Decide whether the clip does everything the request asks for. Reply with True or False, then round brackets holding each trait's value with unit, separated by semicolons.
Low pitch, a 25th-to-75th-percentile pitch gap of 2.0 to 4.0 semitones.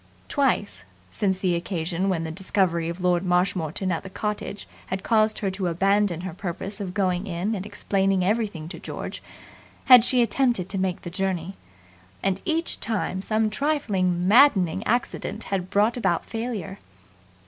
False (195 Hz; 2.9 semitones)